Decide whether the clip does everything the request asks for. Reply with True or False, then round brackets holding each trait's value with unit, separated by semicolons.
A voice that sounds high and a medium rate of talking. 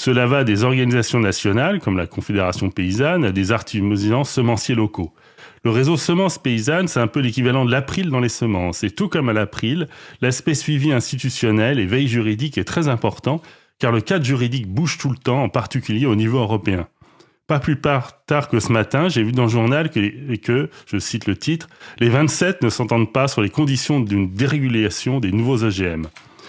False (125 Hz; 195 wpm)